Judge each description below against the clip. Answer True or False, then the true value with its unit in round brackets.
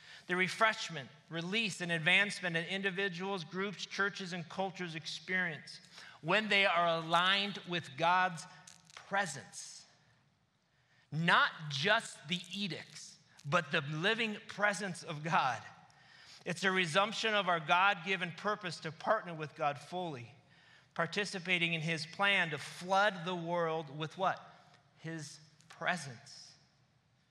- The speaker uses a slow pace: True (120 wpm)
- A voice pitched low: False (175 Hz)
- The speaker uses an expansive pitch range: False (3.4 semitones)